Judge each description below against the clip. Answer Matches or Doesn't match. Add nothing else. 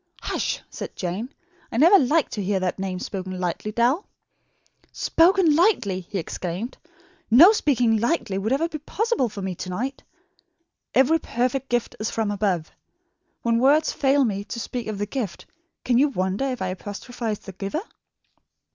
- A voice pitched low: Doesn't match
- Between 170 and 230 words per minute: Doesn't match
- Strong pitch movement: Matches